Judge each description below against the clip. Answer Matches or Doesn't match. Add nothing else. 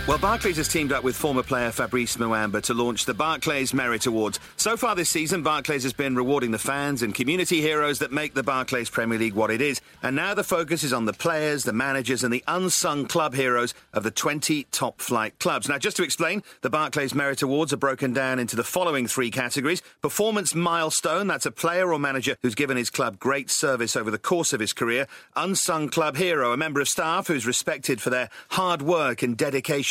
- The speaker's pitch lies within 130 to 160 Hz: Matches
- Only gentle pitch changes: Doesn't match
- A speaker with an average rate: Doesn't match